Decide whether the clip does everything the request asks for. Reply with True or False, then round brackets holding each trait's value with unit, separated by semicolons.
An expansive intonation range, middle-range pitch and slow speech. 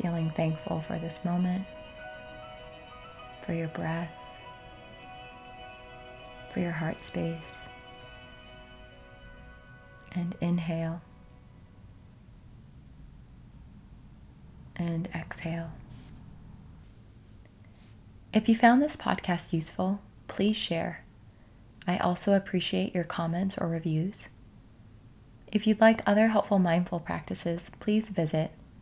True (7.4 semitones; 155 Hz; 85 wpm)